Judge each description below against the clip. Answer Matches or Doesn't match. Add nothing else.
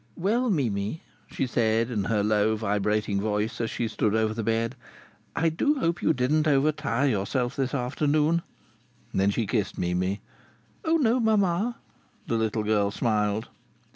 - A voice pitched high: Doesn't match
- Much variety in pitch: Matches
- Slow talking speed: Doesn't match